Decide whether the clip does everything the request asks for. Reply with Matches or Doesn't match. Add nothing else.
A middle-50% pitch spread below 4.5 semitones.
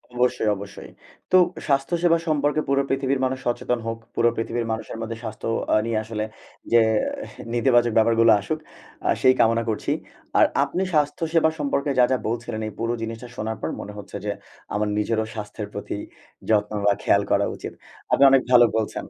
Matches